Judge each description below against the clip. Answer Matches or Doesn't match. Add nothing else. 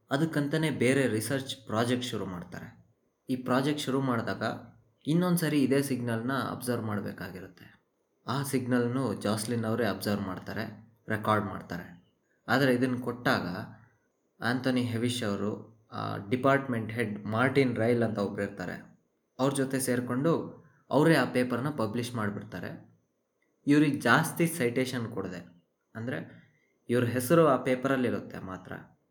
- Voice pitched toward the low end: Matches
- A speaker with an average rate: Doesn't match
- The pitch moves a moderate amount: Matches